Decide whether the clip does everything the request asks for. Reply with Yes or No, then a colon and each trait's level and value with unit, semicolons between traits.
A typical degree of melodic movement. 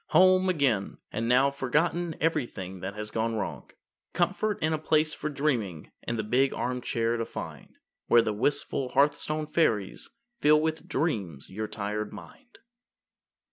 No: wide, 6.2 semitones